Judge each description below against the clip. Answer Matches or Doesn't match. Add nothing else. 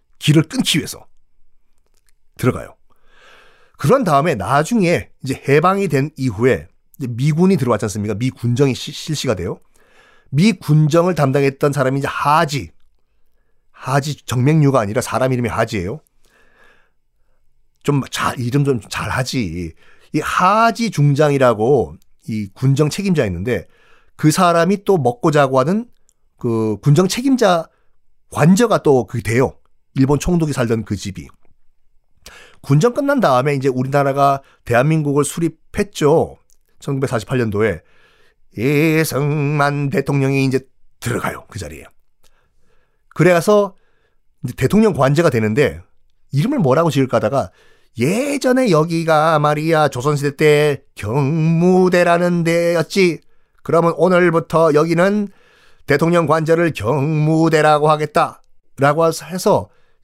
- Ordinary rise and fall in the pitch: Matches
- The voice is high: Doesn't match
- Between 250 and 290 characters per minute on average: Matches